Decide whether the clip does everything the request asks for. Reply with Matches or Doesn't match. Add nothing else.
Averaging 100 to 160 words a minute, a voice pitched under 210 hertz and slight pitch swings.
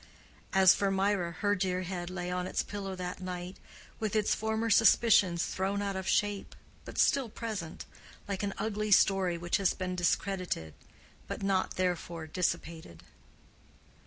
Matches